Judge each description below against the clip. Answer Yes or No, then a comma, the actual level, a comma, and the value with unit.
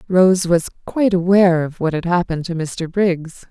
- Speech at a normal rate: Yes, average, 190 wpm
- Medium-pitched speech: Yes, medium, 175 Hz